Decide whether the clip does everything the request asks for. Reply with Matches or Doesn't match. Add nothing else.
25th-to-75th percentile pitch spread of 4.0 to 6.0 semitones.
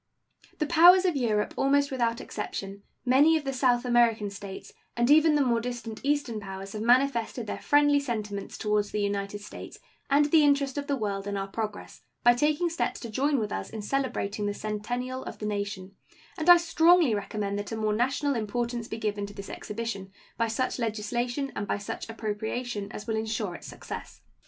Matches